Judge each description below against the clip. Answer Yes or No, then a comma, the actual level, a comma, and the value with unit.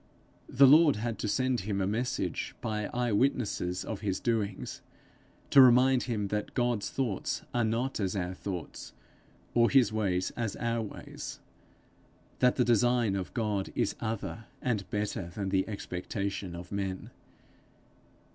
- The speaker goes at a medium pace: Yes, average, 145 wpm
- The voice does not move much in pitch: No, average, 3.7 semitones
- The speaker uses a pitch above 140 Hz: No, low, 110 Hz